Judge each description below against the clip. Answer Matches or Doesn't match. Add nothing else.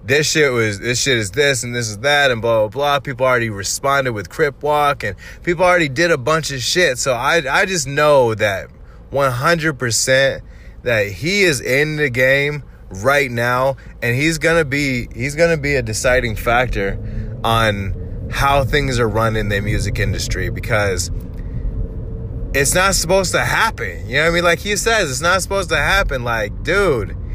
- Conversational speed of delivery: Matches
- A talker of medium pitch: Doesn't match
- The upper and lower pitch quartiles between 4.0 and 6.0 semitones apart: Matches